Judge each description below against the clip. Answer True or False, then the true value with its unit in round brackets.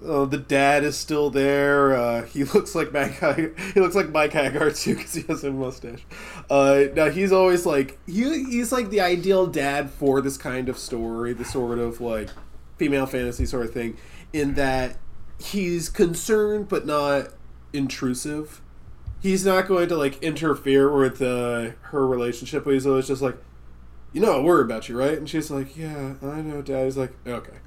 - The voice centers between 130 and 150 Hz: True (140 Hz)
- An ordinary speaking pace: True (185 wpm)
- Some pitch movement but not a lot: True (3.8 semitones)